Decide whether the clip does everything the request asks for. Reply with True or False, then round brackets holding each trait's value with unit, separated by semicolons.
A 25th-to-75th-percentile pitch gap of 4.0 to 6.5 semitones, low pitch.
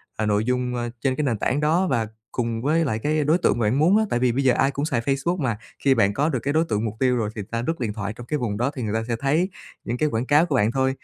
True (4.4 semitones; 130 Hz)